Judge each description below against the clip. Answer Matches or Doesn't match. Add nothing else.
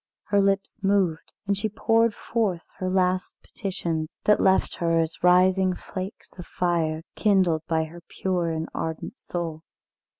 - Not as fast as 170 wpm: Matches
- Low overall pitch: Doesn't match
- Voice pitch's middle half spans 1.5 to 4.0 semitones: Matches